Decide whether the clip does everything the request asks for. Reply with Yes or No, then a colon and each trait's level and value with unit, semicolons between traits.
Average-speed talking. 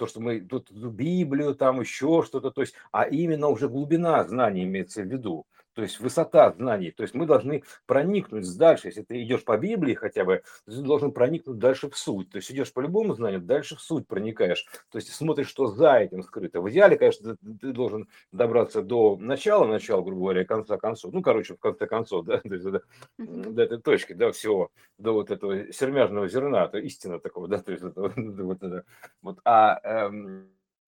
No: fast, 205 wpm